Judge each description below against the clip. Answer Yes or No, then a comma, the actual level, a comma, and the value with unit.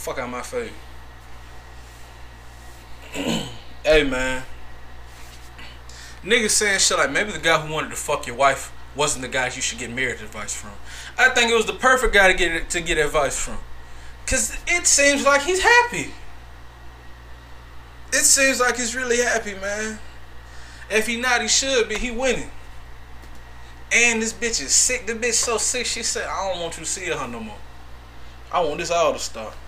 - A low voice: Yes, low, 105 Hz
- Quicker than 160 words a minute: Yes, average, 180 wpm